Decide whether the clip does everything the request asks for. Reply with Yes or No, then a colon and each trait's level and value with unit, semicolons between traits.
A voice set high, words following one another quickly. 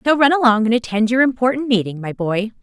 Yes: high, 235 Hz; fast, 230 wpm